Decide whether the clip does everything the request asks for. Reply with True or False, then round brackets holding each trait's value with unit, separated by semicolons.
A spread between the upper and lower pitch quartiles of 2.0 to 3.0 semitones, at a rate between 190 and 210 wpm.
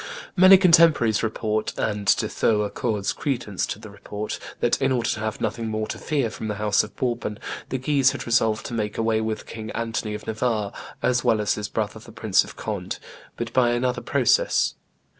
True (2.5 semitones; 195 wpm)